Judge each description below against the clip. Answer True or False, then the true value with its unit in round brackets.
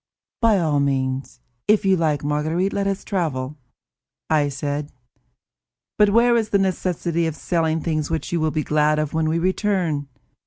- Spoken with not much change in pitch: False (4.1 semitones)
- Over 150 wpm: True (165 wpm)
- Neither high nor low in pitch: True (160 Hz)